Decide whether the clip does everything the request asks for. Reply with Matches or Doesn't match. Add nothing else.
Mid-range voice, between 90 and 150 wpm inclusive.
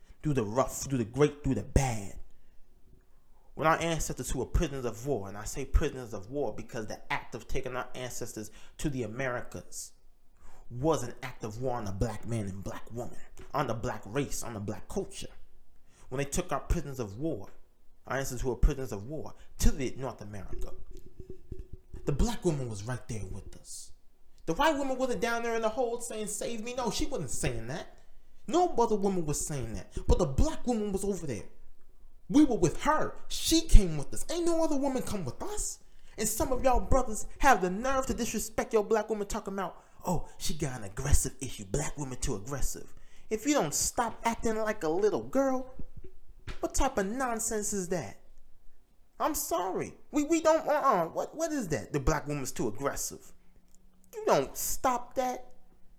Doesn't match